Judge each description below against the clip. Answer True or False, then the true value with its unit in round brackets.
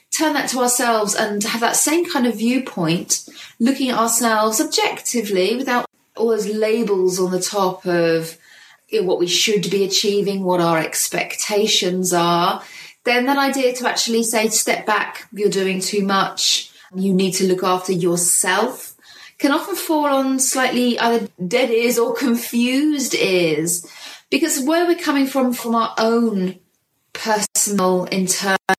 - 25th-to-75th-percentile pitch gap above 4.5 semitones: True (5.0 semitones)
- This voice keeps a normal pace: True (150 wpm)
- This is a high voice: True (220 Hz)